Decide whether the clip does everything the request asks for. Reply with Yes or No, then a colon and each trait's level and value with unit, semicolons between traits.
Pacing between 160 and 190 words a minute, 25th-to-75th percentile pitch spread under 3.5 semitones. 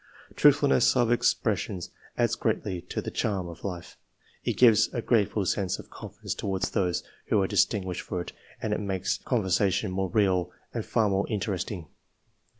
Yes: average, 170 wpm; narrow, 2.6 semitones